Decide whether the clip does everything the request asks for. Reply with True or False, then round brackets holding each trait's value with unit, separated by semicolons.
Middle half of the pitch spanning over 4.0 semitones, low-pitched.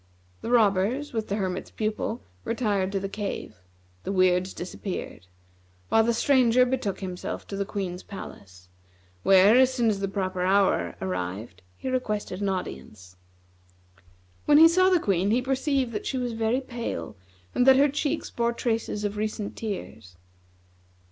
False (4.8 semitones; 210 Hz)